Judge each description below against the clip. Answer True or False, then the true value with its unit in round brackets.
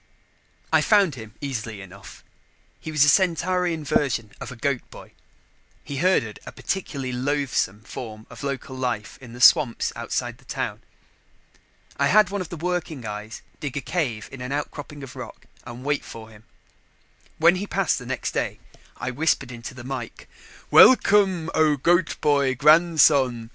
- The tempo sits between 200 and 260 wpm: False (160 wpm)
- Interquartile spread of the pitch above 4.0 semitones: True (5.1 semitones)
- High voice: False (140 Hz)